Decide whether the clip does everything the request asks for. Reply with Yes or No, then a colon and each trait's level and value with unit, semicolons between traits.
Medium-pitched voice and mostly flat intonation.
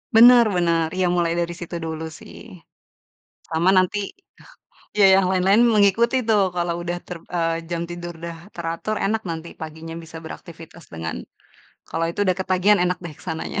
Yes: medium, 175 Hz; narrow, 2.3 semitones